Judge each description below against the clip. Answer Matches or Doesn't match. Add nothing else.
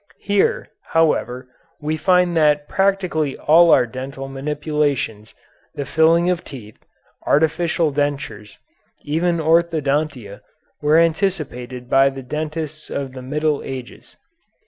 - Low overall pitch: Doesn't match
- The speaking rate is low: Matches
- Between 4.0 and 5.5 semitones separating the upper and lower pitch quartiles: Doesn't match